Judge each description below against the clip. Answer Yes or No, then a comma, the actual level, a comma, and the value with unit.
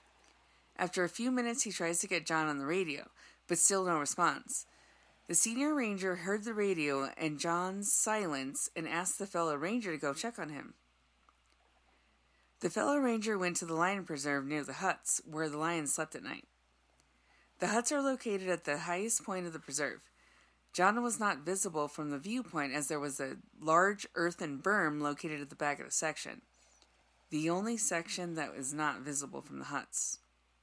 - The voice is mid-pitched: Yes, medium, 165 Hz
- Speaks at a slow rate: No, average, 185 wpm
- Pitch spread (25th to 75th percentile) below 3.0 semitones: No, average, 5.1 semitones